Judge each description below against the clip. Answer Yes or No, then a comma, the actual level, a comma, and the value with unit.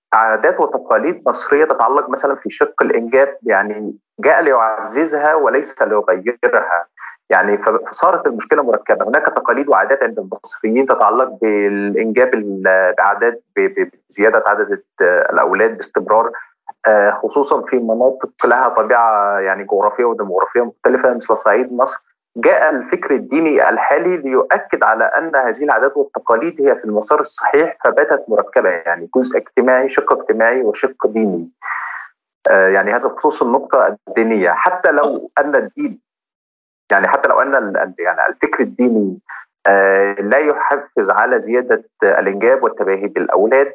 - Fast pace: No, average, 120 wpm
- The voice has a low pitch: Yes, low, 130 Hz